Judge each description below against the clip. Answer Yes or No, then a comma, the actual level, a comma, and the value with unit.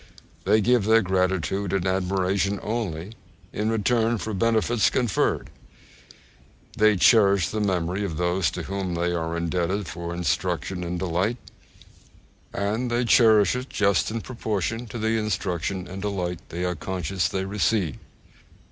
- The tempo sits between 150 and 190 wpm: No, average, 140 wpm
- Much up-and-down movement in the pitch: No, average, 3.6 semitones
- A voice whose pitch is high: No, very low, 95 Hz